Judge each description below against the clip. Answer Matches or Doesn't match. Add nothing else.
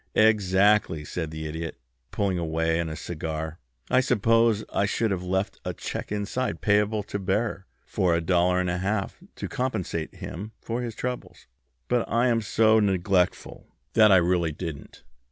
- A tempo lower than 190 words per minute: Matches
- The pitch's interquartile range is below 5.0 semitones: Matches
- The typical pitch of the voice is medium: Doesn't match